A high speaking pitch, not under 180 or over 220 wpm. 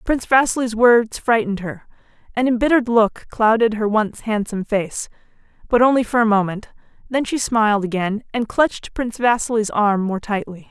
No: high, 225 Hz; average, 165 wpm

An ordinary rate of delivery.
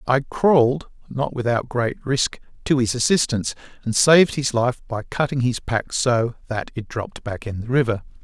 Yes: average, 180 wpm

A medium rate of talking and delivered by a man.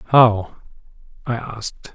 No: slow, 90 wpm; male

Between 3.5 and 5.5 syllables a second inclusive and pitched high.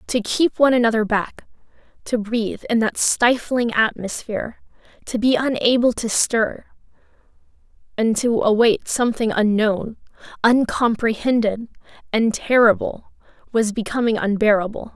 Yes: 4.7 syllables/s; high, 225 Hz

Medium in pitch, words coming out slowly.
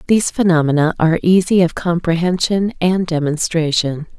Yes: medium, 170 Hz; slow, 115 wpm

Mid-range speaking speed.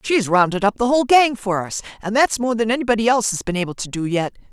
No: fast, 265 wpm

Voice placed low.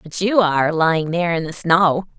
No: medium, 170 Hz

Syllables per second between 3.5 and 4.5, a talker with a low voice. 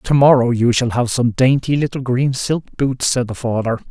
No: 5.0 syllables/s; low, 125 Hz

